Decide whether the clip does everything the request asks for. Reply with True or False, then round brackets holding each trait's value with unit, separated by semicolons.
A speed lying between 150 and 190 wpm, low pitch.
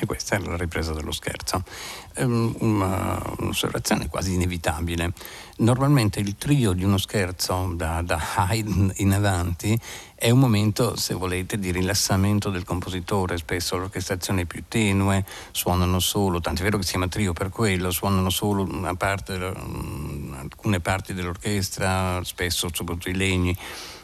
False (135 wpm; 95 Hz)